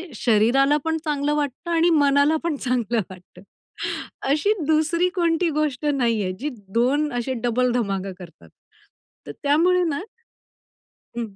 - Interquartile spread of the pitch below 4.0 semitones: No, average, 4.8 semitones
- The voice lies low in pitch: No, very high, 280 Hz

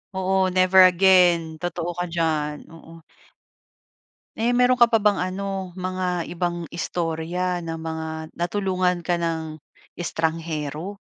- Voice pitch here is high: No, medium, 175 Hz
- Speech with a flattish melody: Yes, narrow, 2.2 semitones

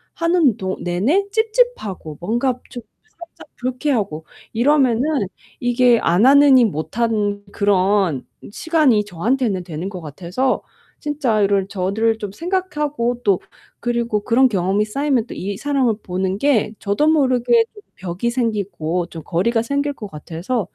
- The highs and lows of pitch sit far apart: Yes, wide, 5.9 semitones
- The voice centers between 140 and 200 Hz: No, high, 230 Hz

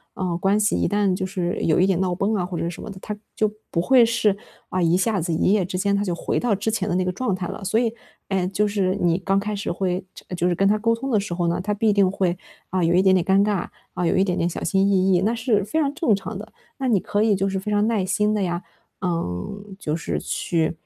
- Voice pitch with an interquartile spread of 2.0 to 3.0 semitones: Yes, narrow, 2.6 semitones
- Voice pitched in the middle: No, high, 195 Hz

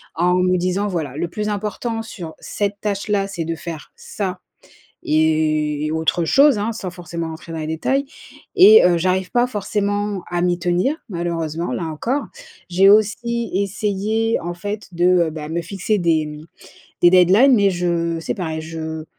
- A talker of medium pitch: Yes, medium, 180 Hz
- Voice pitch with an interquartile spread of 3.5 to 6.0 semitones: Yes, average, 3.9 semitones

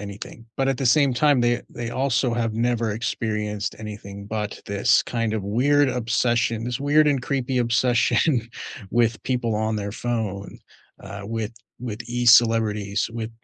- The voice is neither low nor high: No, low, 115 Hz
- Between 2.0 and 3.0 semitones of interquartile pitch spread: Yes, narrow, 2.5 semitones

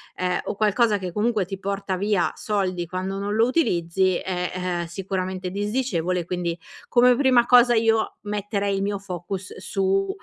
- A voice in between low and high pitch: No, high, 195 Hz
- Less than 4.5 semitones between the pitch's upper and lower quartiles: Yes, narrow, 2.5 semitones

